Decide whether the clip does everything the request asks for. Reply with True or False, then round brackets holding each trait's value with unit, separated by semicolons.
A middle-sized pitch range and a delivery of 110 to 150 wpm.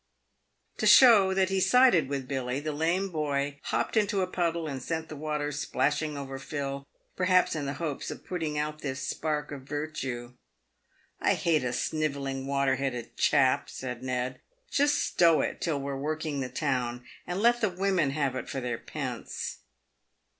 False (3.9 semitones; 175 wpm)